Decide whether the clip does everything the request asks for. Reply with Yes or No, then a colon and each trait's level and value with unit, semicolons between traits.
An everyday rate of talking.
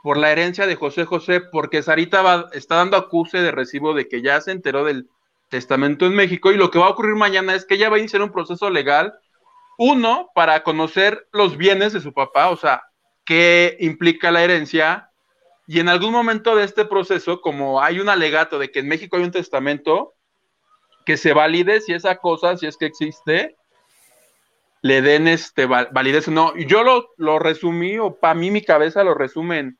No: fast, 195 wpm